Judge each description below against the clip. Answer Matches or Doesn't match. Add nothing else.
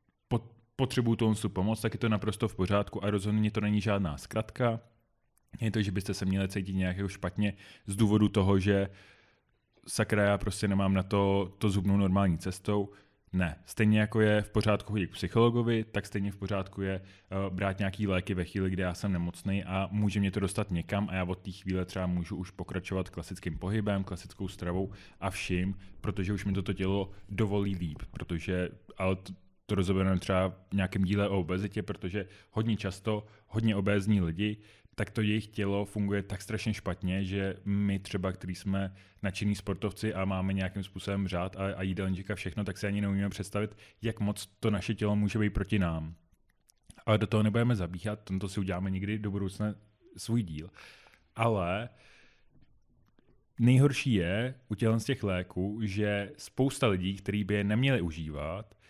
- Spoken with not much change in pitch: Matches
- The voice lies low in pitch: Matches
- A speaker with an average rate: Doesn't match